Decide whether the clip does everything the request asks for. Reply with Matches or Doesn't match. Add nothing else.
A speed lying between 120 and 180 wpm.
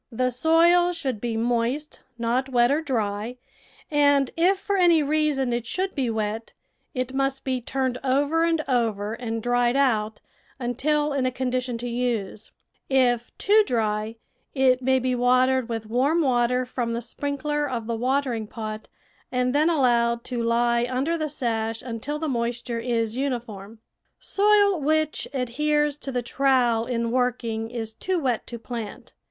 Matches